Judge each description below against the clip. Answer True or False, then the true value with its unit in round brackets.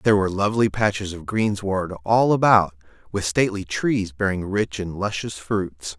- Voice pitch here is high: False (100 Hz)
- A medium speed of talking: True (160 wpm)